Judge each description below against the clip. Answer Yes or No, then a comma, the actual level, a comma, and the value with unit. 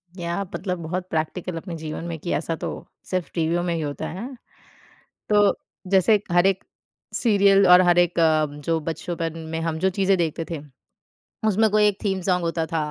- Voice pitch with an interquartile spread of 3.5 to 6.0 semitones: No, average, 2.8 semitones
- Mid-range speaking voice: Yes, medium, 175 Hz